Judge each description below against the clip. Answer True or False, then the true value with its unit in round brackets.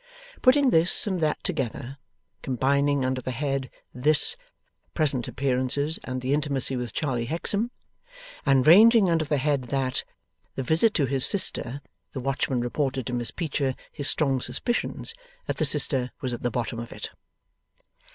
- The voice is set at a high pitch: False (135 Hz)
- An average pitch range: True (3.3 semitones)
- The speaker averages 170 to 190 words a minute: False (155 wpm)